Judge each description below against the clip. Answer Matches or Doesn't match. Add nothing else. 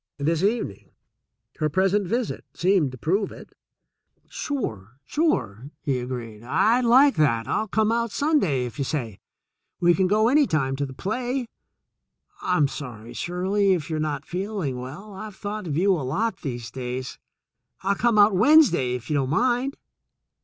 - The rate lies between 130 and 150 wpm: Doesn't match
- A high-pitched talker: Doesn't match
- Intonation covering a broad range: Matches